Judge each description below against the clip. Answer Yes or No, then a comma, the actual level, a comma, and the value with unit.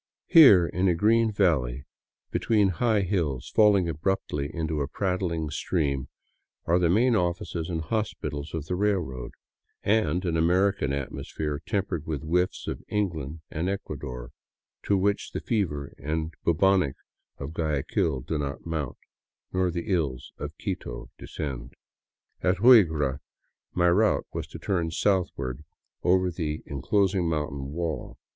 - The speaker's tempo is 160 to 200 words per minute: No, average, 140 wpm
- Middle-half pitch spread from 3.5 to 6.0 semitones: Yes, average, 4.7 semitones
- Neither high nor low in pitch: No, very low, 85 Hz